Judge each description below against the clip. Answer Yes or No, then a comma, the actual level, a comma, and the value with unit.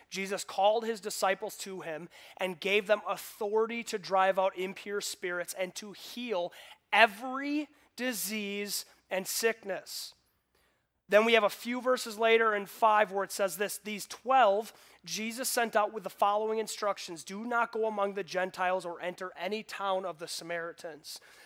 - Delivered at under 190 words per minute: Yes, average, 160 wpm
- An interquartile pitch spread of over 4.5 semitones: No, average, 3.0 semitones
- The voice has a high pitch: Yes, high, 205 Hz